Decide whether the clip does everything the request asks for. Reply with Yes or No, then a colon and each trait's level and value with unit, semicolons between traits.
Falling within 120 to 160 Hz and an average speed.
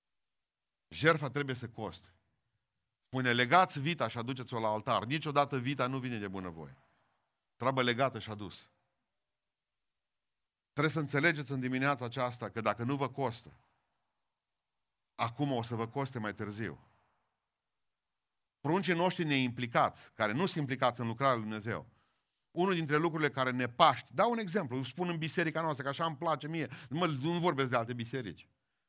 Yes: low, 135 Hz; average, 155 wpm